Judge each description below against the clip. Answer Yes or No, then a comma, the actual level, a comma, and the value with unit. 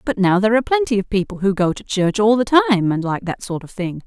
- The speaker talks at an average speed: No, fast, 295 wpm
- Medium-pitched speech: No, high, 210 Hz